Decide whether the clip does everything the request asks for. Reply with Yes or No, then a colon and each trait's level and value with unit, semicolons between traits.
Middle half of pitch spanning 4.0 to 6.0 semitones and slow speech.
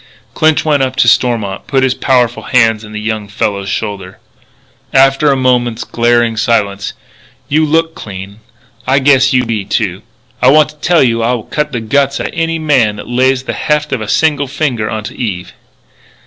No: average, 4.4 semitones; average, 175 wpm